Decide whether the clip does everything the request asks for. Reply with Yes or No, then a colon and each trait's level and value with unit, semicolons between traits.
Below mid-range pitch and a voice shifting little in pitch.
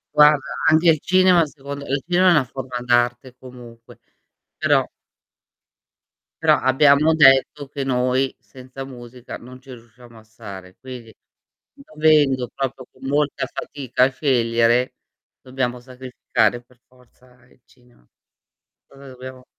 Yes: low, 130 Hz; narrow, 2.3 semitones